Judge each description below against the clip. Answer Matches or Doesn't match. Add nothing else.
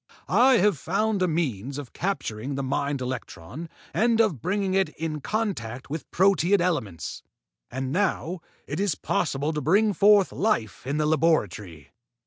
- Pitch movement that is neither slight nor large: Doesn't match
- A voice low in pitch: Doesn't match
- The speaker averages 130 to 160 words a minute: Matches